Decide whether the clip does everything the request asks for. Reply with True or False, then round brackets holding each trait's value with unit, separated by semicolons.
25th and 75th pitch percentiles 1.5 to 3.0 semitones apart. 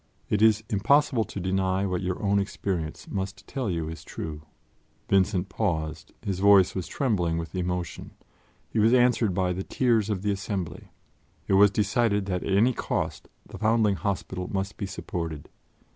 True (2.6 semitones)